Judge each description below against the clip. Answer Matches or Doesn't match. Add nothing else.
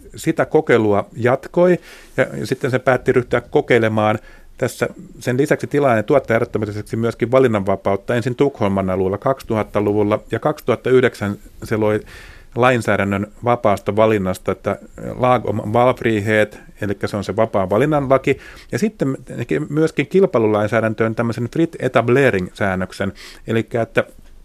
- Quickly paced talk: Doesn't match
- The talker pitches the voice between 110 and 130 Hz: Matches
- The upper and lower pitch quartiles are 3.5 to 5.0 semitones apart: Matches